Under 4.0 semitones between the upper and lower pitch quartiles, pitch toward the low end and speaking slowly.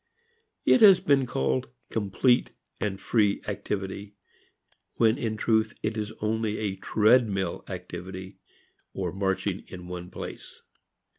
Yes: average, 2.7 semitones; low, 105 Hz; slow, 120 wpm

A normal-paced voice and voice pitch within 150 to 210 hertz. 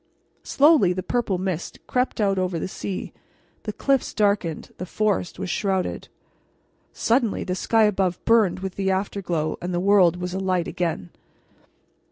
Yes: average, 150 wpm; high, 190 Hz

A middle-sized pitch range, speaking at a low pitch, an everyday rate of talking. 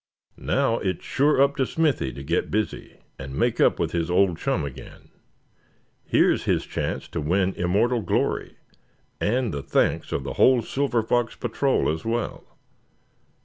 No: wide, 7.2 semitones; low, 105 Hz; average, 155 wpm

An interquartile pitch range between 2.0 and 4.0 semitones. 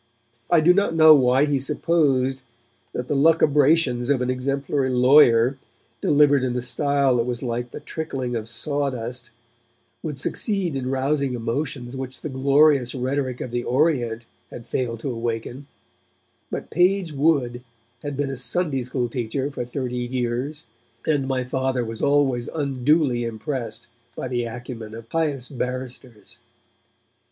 Yes: average, 2.9 semitones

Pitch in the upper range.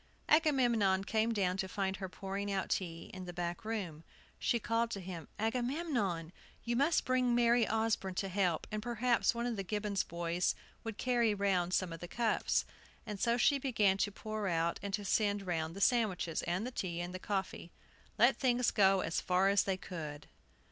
Yes: high, 200 Hz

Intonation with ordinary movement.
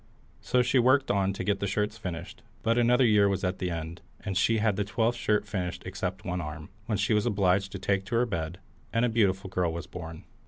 Yes: average, 3.8 semitones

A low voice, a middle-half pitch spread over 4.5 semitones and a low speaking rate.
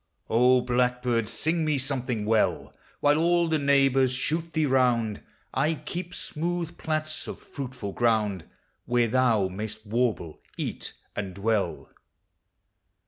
Yes: low, 125 Hz; wide, 5.4 semitones; slow, 125 wpm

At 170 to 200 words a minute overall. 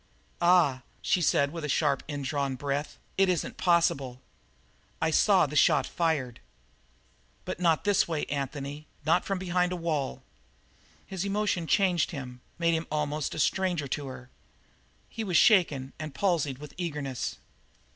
No: average, 145 wpm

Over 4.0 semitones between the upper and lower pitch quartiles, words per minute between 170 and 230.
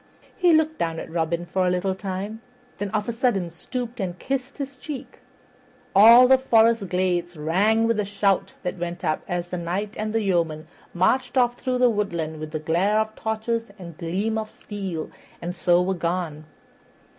Yes: average, 4.6 semitones; average, 180 wpm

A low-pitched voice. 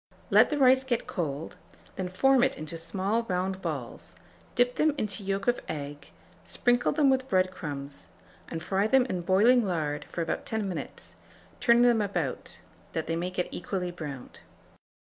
No: high, 190 Hz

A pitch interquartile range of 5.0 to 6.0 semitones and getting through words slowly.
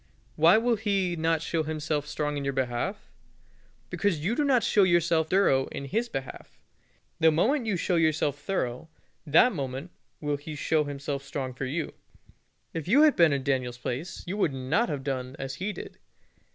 No: wide, 5.4 semitones; average, 180 wpm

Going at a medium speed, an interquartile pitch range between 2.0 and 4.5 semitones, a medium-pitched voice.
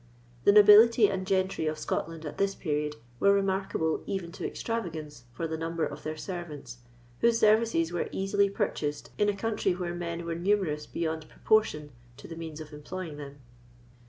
Yes: average, 170 wpm; average, 4.2 semitones; medium, 170 Hz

